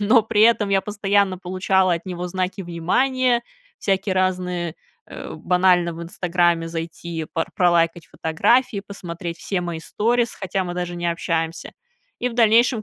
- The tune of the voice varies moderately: Yes, average, 3.1 semitones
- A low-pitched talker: No, medium, 185 Hz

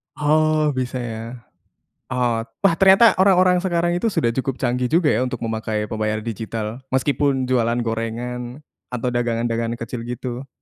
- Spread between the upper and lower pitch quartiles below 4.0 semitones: No, average, 4.4 semitones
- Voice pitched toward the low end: Yes, low, 125 Hz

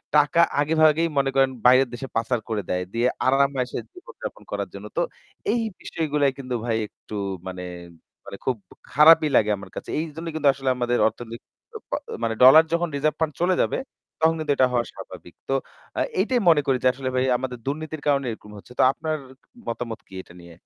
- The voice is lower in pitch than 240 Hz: Yes, low, 135 Hz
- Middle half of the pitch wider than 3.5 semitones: Yes, average, 4.4 semitones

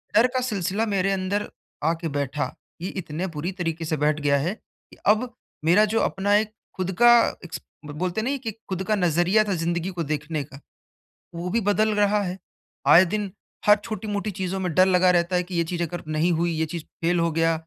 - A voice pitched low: No, medium, 180 Hz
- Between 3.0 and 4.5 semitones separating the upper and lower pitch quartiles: Yes, average, 3.7 semitones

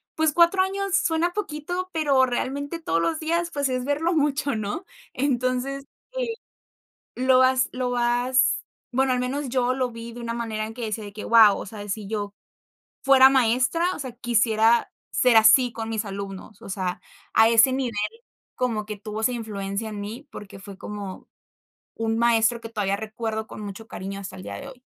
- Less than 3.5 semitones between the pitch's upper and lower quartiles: No, average, 4.0 semitones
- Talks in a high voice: Yes, high, 240 Hz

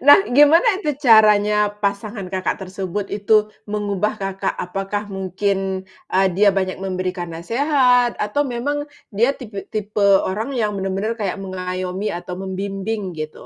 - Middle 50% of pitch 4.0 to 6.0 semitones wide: No, narrow, 2.5 semitones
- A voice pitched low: No, high, 200 Hz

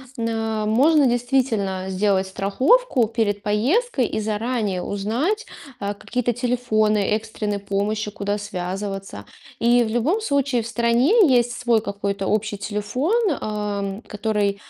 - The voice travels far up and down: No, average, 3.2 semitones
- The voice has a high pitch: Yes, high, 220 Hz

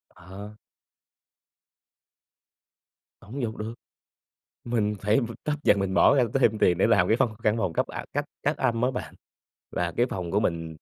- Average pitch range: Yes, average, 3.8 semitones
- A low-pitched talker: Yes, low, 105 Hz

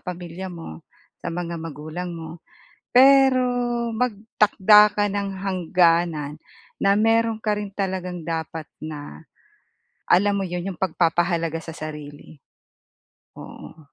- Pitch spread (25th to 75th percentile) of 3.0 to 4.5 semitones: Yes, average, 3.8 semitones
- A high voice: No, medium, 175 Hz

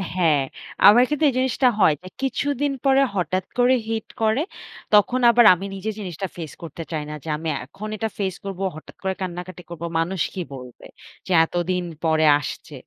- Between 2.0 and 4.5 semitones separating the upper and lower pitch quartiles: No, average, 5.0 semitones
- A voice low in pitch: No, medium, 185 Hz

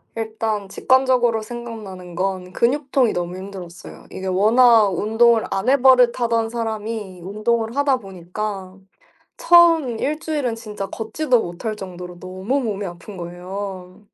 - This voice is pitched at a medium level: No, high, 215 Hz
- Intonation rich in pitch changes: No, average, 4.2 semitones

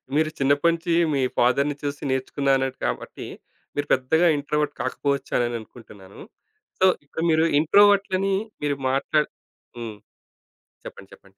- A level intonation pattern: No, average, 3.4 semitones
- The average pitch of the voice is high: No, medium, 145 Hz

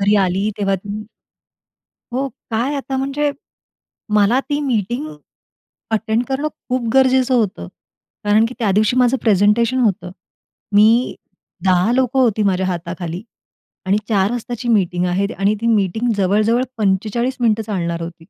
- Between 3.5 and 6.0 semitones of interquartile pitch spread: Yes, average, 4.1 semitones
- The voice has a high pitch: Yes, high, 215 Hz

